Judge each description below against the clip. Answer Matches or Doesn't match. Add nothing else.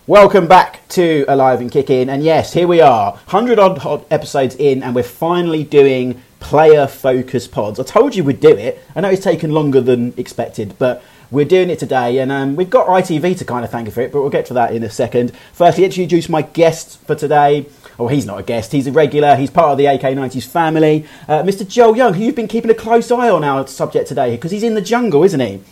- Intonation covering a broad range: Matches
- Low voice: Doesn't match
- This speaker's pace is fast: Matches